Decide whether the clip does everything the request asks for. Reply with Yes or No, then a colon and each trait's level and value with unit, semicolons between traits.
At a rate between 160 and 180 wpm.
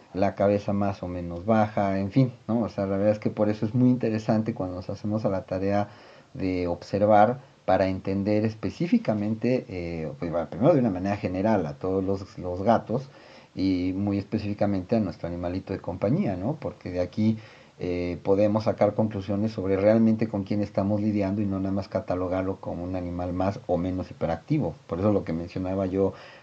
No: fast, 190 wpm